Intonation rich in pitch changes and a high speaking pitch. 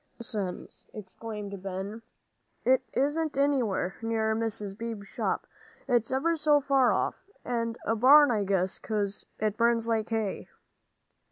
No: average, 3.9 semitones; high, 225 Hz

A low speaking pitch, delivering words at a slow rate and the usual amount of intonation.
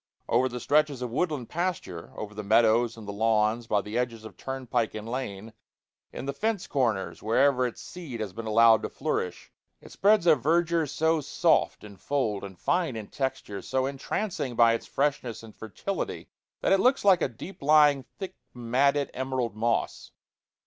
No: low, 125 Hz; average, 175 wpm; average, 5.0 semitones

